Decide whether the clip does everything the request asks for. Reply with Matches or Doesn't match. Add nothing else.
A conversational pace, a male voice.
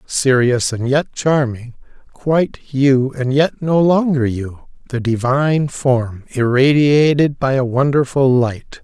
Doesn't match